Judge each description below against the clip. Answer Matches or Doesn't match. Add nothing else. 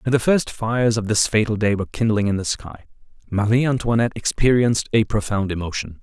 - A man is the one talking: Matches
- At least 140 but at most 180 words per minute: Doesn't match